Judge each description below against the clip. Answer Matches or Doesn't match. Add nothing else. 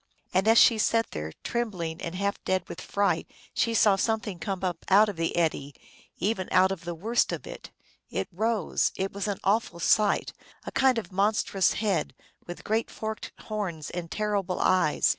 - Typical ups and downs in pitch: Matches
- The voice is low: Doesn't match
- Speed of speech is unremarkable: Matches